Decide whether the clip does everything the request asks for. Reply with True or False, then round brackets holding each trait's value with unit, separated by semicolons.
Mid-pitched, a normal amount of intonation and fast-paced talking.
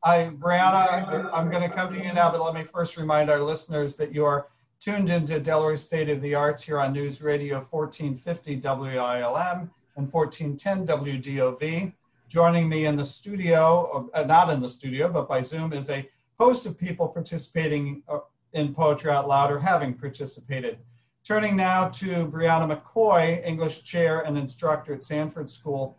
False (155 Hz; 3.0 semitones; 165 wpm)